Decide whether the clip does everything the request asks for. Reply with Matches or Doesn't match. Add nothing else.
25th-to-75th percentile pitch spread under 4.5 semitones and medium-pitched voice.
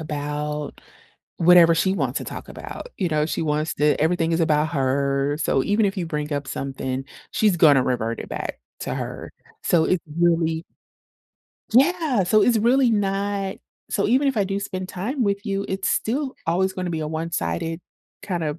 Doesn't match